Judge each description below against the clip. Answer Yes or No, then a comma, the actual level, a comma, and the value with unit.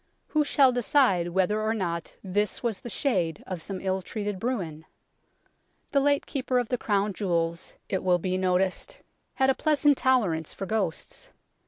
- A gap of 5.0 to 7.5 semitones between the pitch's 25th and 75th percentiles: Yes, wide, 5.6 semitones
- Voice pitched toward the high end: Yes, high, 200 Hz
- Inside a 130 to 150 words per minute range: No, average, 165 wpm